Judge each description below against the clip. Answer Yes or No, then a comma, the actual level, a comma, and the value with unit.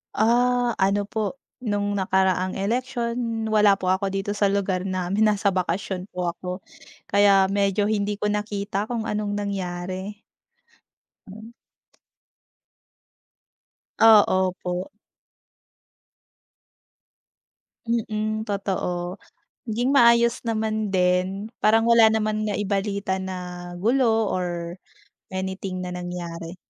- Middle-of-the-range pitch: No, high, 200 Hz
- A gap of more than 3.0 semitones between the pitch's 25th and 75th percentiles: No, average, 2.7 semitones